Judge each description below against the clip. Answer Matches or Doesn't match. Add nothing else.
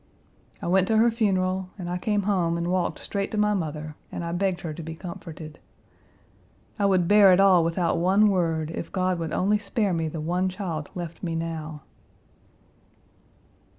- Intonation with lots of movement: Doesn't match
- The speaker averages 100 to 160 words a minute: Doesn't match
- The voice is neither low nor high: Matches